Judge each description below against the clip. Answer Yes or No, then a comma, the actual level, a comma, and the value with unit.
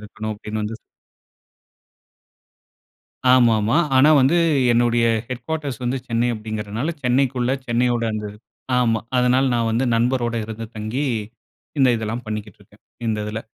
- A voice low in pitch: Yes, low, 115 Hz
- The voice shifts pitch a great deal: No, narrow, 2.5 semitones